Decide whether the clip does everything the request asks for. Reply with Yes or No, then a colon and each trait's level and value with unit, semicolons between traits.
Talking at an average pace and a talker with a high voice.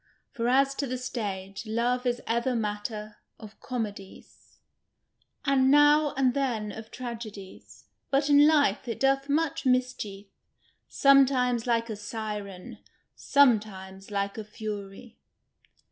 No: slow, 120 wpm; high, 235 Hz